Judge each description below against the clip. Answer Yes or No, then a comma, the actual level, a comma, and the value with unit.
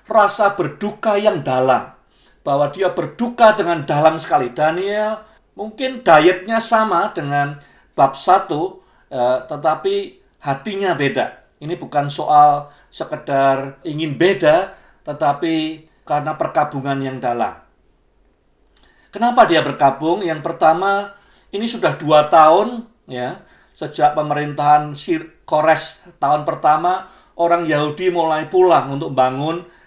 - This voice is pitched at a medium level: Yes, medium, 160 Hz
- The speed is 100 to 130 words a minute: Yes, average, 105 wpm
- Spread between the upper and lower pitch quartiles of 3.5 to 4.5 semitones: No, average, 5.3 semitones